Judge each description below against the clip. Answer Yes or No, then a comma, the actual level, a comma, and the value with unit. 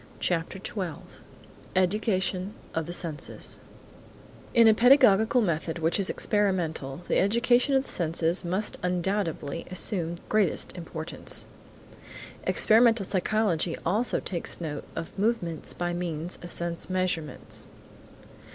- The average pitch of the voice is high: No, medium, 180 Hz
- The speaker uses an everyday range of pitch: Yes, average, 4.0 semitones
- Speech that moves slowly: Yes, slow, 115 wpm